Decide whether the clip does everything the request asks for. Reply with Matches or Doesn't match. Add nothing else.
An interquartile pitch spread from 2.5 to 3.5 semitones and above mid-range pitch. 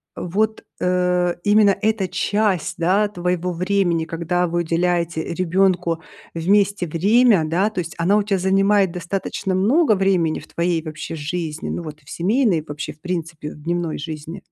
Doesn't match